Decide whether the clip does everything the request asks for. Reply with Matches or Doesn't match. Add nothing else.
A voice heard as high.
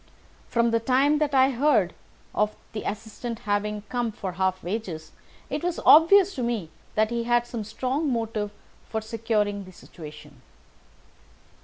Matches